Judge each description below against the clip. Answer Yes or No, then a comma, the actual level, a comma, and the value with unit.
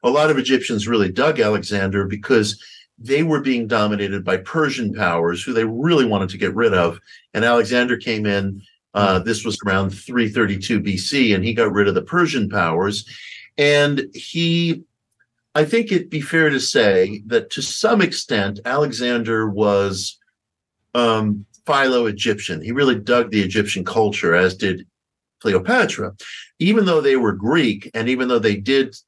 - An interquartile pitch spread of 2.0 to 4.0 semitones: No, average, 5.0 semitones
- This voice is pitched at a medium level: No, low, 115 Hz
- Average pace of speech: Yes, average, 160 wpm